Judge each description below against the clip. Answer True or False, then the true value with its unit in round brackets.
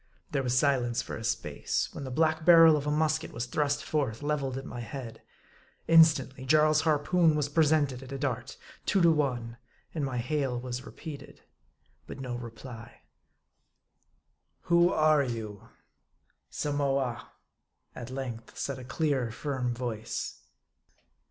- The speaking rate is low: False (150 wpm)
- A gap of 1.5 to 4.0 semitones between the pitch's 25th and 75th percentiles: True (3.7 semitones)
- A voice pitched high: False (135 Hz)